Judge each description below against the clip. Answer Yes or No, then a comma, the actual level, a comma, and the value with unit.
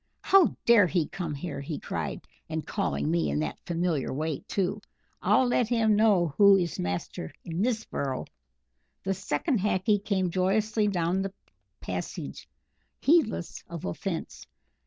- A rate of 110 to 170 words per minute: Yes, average, 145 wpm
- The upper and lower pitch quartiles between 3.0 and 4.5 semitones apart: No, average, 5.3 semitones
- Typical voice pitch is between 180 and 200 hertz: Yes, medium, 185 Hz